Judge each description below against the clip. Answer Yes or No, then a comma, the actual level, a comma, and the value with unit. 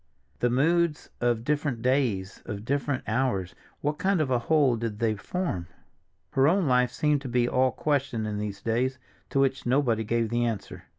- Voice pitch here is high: No, low, 125 Hz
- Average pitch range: Yes, average, 4.0 semitones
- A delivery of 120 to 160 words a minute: No, average, 180 wpm